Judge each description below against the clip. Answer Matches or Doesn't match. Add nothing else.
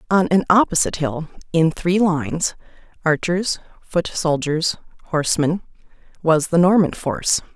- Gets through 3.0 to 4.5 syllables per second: Doesn't match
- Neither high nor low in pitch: Matches